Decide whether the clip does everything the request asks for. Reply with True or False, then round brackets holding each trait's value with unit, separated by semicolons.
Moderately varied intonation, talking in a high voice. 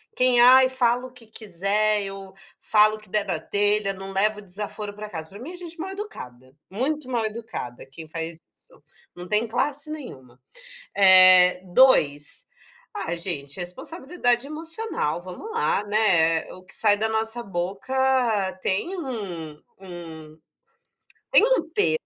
False (6.2 semitones; 210 Hz)